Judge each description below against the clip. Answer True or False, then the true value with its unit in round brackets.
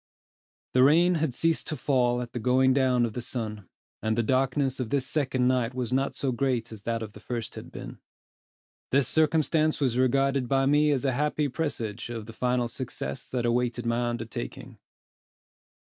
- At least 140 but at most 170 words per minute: False (185 wpm)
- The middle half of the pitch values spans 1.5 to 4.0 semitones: True (2.6 semitones)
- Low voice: True (125 Hz)